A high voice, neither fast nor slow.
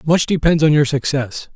No: medium, 145 Hz; average, 195 wpm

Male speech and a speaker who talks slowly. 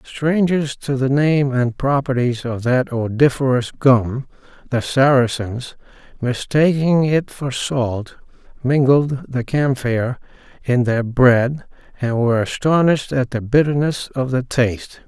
Yes: male; slow, 125 wpm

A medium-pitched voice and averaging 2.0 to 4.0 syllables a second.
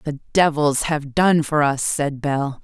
Yes: medium, 145 Hz; 3.5 syllables/s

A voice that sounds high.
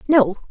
Yes: high, 240 Hz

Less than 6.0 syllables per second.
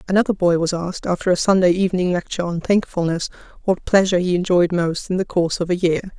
No: 6.7 syllables/s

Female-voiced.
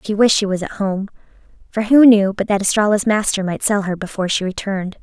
Yes: female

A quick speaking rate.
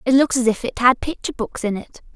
Yes: fast, 280 wpm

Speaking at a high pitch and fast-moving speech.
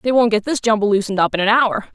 Yes: high, 220 Hz; fast, 310 wpm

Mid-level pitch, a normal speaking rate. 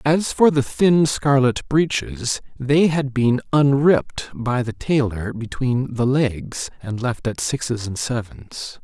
No: low, 130 Hz; average, 150 wpm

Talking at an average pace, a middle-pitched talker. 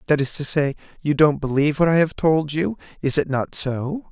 No: fast, 235 wpm; medium, 145 Hz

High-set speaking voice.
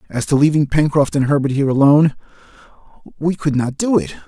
No: medium, 145 Hz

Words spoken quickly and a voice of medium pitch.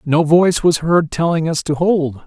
Yes: fast, 210 wpm; medium, 160 Hz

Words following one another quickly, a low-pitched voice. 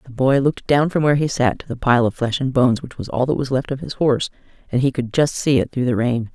Yes: fast, 310 wpm; low, 130 Hz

